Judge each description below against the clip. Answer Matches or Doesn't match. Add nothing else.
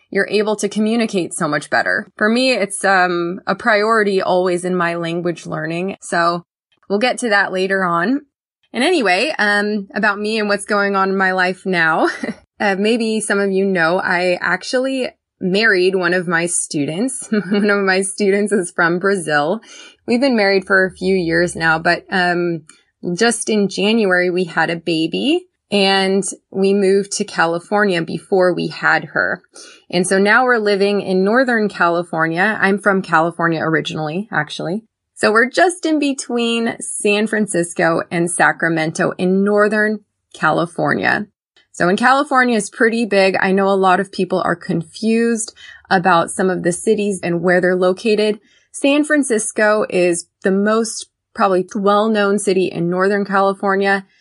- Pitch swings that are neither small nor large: Matches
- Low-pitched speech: Doesn't match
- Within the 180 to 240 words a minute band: Doesn't match